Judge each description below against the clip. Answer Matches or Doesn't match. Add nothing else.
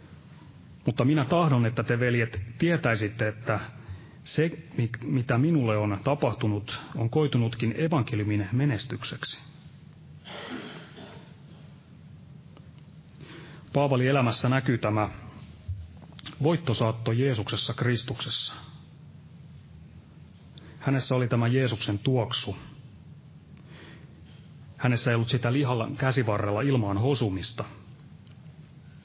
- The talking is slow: Matches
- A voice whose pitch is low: Matches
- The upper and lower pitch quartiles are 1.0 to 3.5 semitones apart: Doesn't match